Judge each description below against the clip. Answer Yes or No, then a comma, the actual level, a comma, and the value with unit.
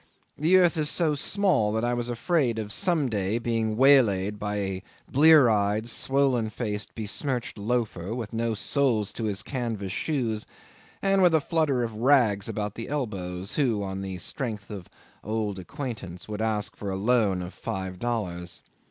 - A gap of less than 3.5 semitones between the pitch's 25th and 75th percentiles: No, average, 4.6 semitones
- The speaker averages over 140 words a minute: Yes, average, 170 wpm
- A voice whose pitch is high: No, low, 110 Hz